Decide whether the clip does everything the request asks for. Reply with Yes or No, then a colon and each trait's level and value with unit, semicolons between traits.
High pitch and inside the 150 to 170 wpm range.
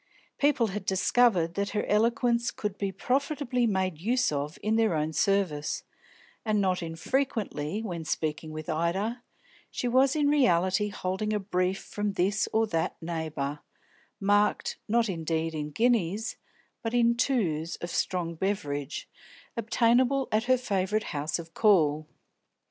No: high, 200 Hz; average, 140 wpm